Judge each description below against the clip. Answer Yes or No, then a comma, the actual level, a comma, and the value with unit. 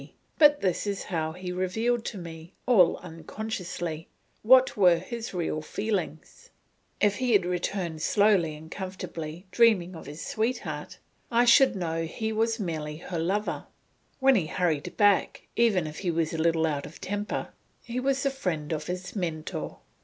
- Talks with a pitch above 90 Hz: Yes, medium, 185 Hz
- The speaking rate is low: No, average, 160 wpm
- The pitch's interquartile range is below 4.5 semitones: No, average, 5.1 semitones